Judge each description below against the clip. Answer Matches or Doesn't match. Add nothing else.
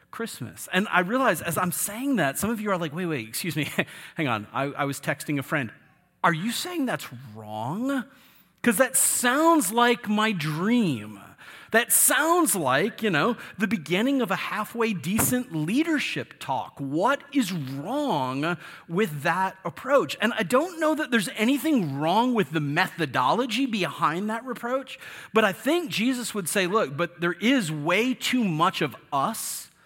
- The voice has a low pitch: Doesn't match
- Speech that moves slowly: Doesn't match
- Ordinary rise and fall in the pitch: Doesn't match